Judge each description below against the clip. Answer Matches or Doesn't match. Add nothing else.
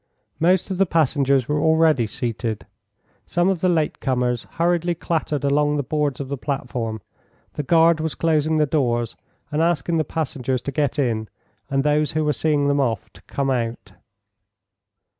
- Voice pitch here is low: Doesn't match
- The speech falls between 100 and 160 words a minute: Doesn't match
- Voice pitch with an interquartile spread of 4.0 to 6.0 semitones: Doesn't match